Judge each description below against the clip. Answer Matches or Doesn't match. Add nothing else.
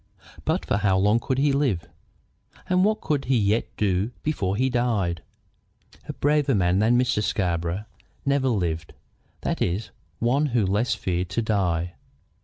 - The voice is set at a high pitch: Doesn't match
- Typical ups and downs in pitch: Doesn't match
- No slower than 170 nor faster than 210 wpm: Doesn't match